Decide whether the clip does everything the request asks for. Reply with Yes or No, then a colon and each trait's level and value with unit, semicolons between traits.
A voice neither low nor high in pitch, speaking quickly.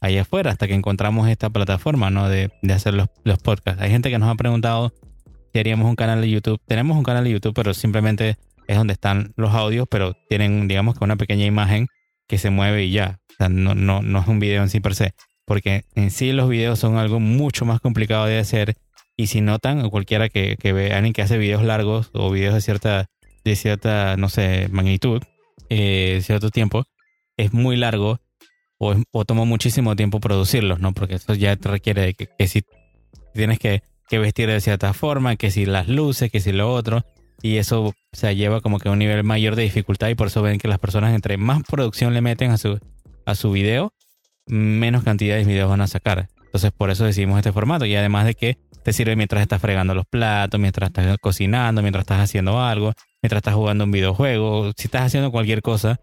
No: low, 105 Hz; fast, 220 wpm